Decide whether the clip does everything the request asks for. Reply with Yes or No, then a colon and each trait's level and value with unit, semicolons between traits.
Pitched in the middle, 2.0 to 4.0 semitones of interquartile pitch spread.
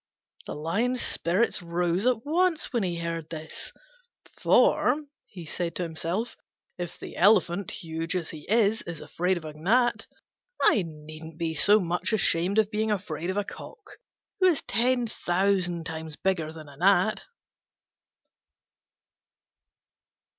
No: medium, 180 Hz; average, 4.7 semitones